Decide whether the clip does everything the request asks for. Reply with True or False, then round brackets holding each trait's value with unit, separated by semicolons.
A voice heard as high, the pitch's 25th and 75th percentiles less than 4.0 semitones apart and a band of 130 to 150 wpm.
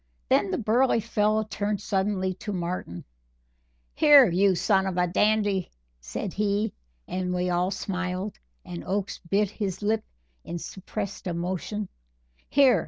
True (195 Hz; 2.7 semitones; 135 wpm)